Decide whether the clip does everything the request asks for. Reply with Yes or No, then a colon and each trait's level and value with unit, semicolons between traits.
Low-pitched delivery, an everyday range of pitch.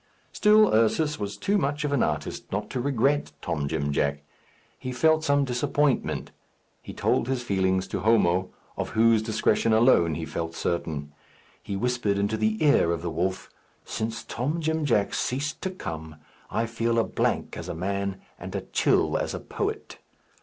No: low, 110 Hz; wide, 7.2 semitones